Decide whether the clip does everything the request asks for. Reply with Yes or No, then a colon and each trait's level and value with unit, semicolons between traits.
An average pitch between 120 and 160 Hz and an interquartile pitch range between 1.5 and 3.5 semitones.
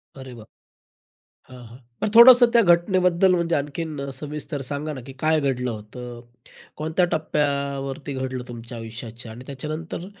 No: medium, 140 Hz; average, 4.2 semitones